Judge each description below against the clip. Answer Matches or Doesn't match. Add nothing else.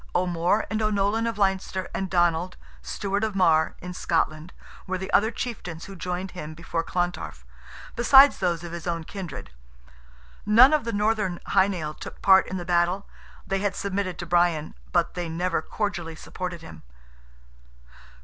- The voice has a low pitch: Doesn't match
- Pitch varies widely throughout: Doesn't match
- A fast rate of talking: Doesn't match